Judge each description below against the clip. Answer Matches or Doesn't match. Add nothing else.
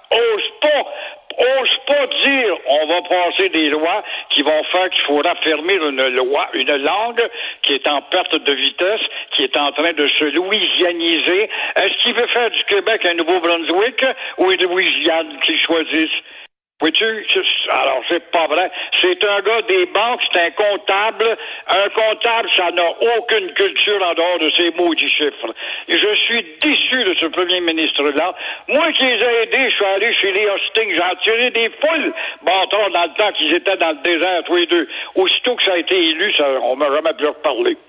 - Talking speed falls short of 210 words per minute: Matches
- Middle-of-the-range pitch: Doesn't match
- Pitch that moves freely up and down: Matches